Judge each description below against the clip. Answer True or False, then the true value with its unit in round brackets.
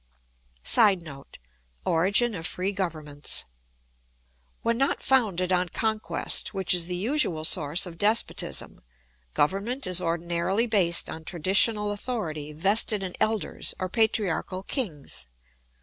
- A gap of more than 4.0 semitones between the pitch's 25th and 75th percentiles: True (4.5 semitones)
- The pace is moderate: False (115 wpm)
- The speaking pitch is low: False (185 Hz)